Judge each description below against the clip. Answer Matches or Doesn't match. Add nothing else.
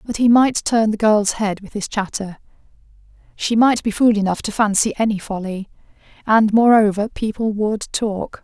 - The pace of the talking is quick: Doesn't match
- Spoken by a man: Doesn't match